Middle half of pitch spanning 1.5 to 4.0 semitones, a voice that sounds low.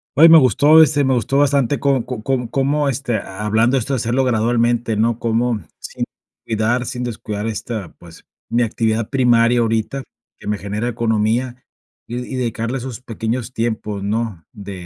Yes: narrow, 2.6 semitones; low, 120 Hz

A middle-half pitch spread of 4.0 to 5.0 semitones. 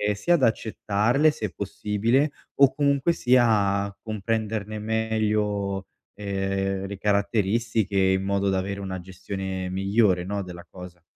No: narrow, 2.4 semitones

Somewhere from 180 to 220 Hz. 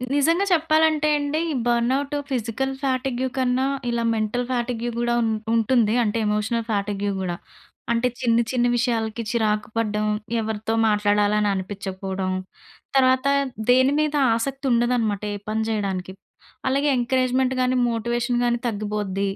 No: high, 235 Hz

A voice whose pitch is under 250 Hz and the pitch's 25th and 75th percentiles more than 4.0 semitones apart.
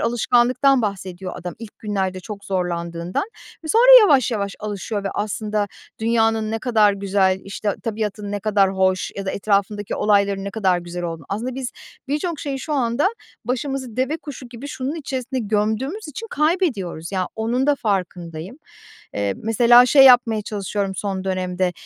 Yes: high, 210 Hz; average, 4.7 semitones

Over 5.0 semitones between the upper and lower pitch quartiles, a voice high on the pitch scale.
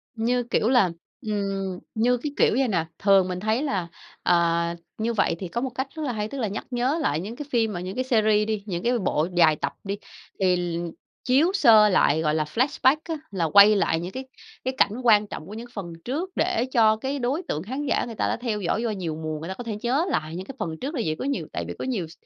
Yes: wide, 5.6 semitones; high, 215 Hz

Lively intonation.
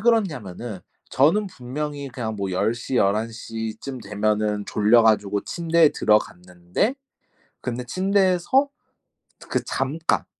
Yes: wide, 7.3 semitones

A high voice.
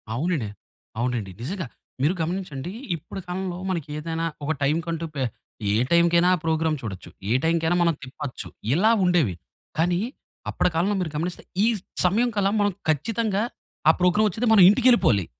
No: medium, 170 Hz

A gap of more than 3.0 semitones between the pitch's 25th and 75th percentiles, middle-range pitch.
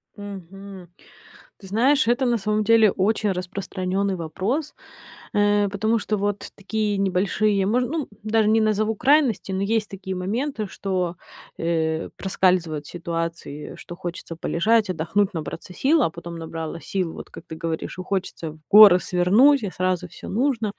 No: average, 3.4 semitones; high, 195 Hz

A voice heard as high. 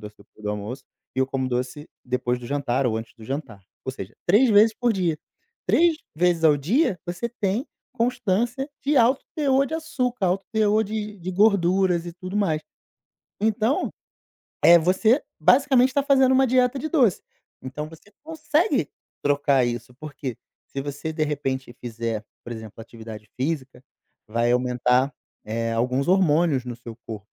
No: medium, 160 Hz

